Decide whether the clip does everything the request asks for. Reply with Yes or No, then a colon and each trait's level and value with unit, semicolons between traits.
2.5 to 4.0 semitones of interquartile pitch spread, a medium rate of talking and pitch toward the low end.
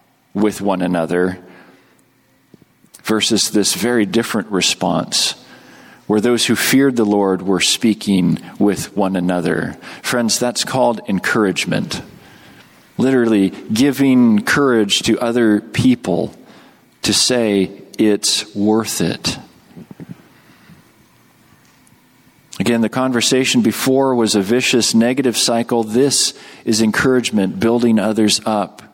No: average, 3.1 semitones; slow, 100 wpm; low, 110 Hz